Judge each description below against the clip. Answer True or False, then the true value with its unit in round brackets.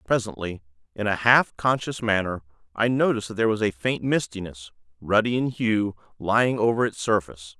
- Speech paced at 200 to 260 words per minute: False (165 wpm)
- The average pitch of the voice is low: True (105 Hz)